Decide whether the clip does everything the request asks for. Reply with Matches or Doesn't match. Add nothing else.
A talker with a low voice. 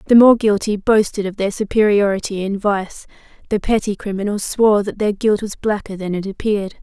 Doesn't match